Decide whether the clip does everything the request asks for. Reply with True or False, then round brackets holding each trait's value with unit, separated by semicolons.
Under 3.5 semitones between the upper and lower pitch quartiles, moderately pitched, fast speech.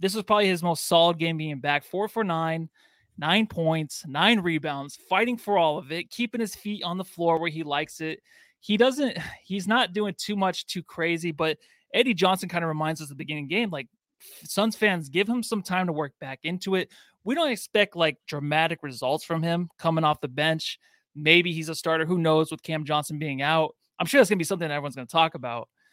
False (4.5 semitones; 170 Hz; 230 wpm)